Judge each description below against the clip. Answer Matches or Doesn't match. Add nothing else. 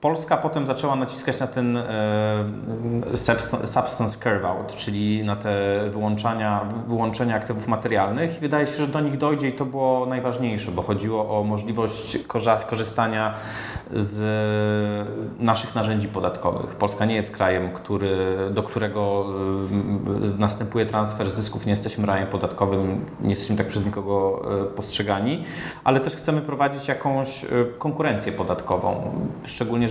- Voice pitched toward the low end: Matches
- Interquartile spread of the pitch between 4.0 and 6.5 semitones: Doesn't match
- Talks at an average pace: Matches